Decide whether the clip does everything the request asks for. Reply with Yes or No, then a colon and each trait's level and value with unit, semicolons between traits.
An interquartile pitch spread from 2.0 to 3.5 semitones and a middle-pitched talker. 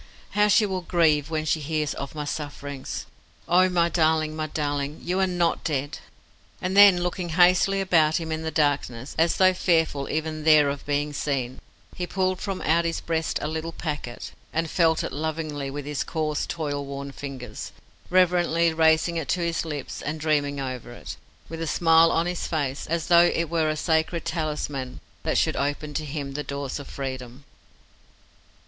Yes: average, 2.8 semitones; medium, 155 Hz